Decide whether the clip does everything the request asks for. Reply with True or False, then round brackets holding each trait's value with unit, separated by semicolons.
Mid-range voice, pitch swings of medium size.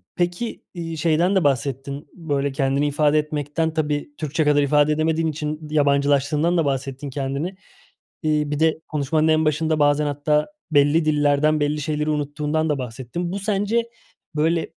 False (150 Hz; 1.9 semitones)